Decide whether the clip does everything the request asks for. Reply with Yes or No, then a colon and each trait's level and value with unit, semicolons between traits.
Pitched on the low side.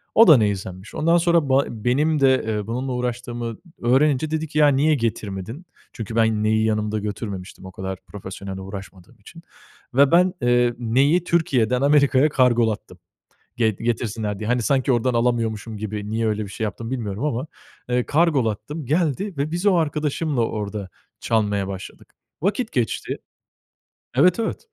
Yes: low, 120 Hz